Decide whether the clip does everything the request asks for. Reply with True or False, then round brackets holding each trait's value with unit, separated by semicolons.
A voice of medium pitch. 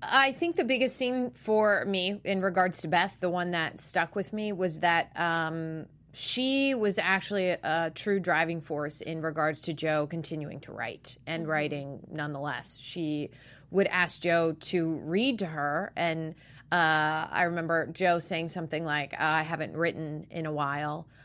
True (165 Hz)